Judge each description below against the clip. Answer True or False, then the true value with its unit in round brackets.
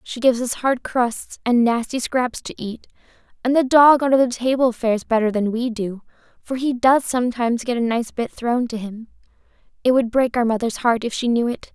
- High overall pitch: True (240 Hz)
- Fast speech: True (215 wpm)